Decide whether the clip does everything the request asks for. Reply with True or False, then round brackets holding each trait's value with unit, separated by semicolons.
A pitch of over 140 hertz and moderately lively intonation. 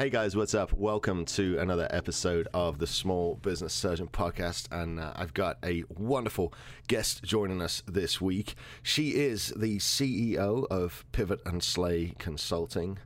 False (95 Hz; 3.8 semitones)